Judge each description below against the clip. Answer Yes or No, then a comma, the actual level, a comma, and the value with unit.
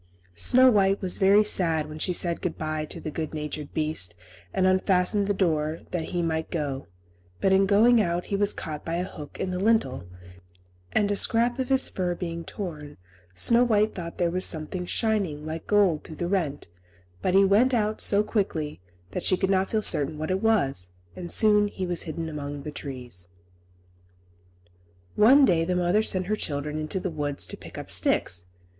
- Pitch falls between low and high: Yes, medium, 180 Hz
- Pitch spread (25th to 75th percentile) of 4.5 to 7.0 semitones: Yes, average, 4.8 semitones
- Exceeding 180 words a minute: Yes, average, 195 wpm